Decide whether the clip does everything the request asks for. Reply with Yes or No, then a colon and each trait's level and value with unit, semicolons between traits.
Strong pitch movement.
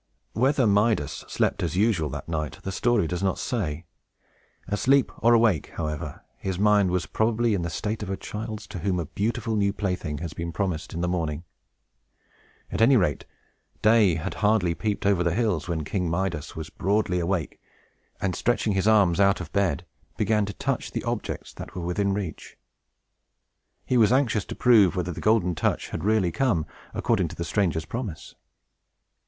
No: average, 4.3 semitones